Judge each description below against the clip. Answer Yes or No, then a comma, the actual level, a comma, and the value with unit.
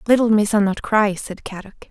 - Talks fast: No, average, 190 wpm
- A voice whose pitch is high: Yes, high, 210 Hz